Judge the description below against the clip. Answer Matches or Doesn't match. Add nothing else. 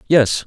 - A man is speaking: Matches